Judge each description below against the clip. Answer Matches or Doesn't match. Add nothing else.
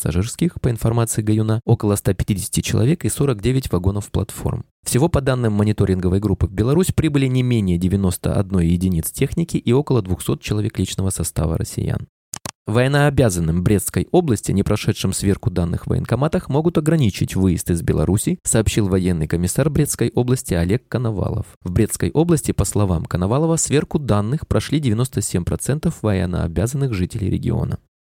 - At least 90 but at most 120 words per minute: Doesn't match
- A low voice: Matches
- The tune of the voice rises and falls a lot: Matches